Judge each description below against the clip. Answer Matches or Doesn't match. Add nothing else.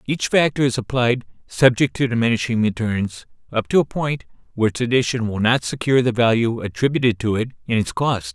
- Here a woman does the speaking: Doesn't match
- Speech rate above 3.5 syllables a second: Matches